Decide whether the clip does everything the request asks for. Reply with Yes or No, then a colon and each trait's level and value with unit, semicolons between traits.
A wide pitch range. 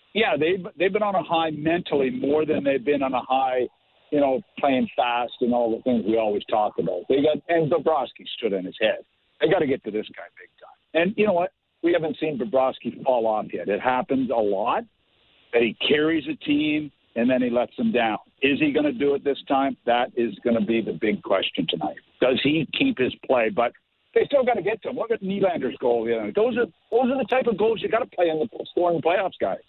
Yes: wide, 7.4 semitones